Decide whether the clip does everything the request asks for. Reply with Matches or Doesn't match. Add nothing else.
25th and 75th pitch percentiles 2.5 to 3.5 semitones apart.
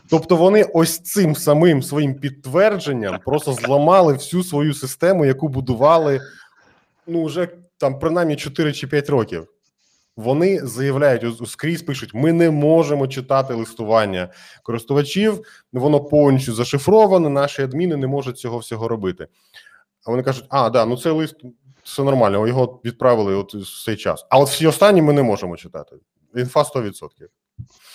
Doesn't match